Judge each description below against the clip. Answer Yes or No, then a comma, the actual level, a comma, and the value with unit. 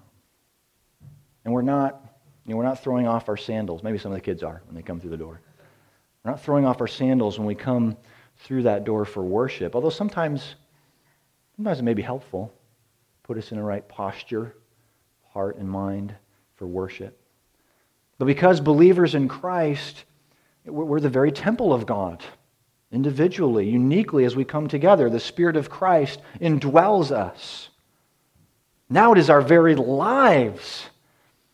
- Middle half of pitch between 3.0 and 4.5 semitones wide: No, wide, 5.4 semitones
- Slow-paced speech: No, average, 160 wpm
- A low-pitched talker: Yes, low, 130 Hz